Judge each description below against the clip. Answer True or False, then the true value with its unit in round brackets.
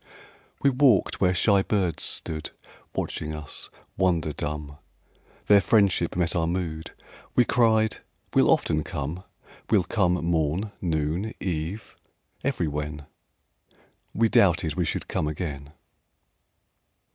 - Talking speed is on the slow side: True (110 wpm)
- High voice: False (85 Hz)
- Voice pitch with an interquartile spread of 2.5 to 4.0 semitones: False (4.6 semitones)